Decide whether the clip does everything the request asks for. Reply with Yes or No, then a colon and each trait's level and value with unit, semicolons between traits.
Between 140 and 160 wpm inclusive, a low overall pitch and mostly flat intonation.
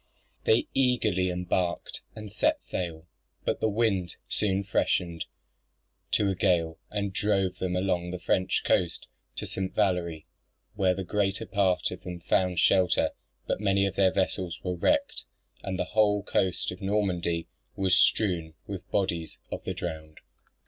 Yes: average, 155 wpm; very low, 95 Hz; narrow, 2.1 semitones